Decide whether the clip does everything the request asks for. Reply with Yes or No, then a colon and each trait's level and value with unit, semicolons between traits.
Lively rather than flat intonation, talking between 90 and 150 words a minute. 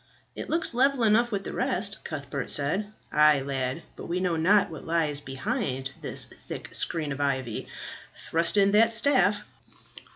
No: wide, 6.9 semitones; average, 160 wpm